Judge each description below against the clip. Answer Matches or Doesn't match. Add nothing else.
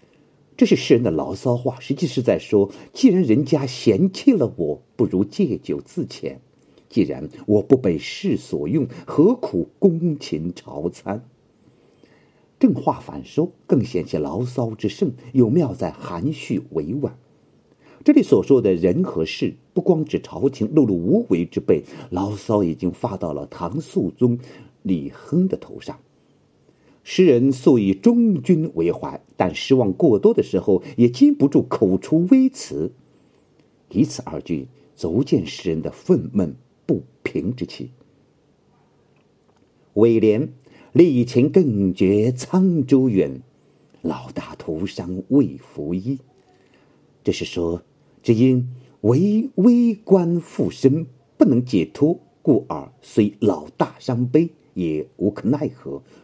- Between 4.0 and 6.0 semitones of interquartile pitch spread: Doesn't match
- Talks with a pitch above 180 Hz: Doesn't match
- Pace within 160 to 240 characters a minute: Matches